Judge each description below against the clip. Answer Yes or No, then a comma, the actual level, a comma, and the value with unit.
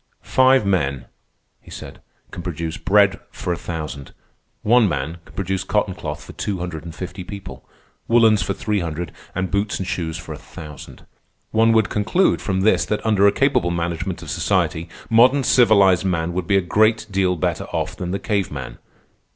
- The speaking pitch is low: Yes, very low, 95 Hz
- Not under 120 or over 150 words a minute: No, average, 185 wpm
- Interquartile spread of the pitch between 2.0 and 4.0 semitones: Yes, average, 3.7 semitones